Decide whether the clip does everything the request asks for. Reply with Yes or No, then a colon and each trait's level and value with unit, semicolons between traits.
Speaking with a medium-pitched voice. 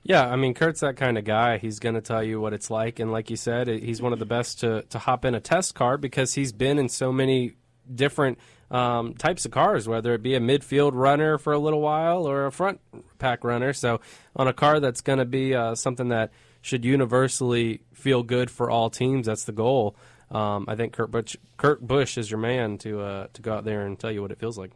No: low, 125 Hz